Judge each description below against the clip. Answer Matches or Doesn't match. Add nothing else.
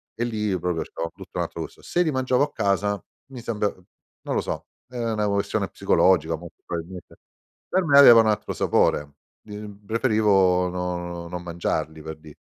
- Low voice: Matches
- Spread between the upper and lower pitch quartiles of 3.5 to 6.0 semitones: Matches